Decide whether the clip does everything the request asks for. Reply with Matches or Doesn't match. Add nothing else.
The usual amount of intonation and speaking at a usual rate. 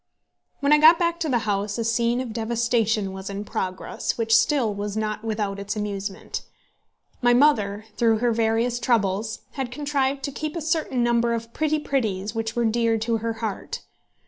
Matches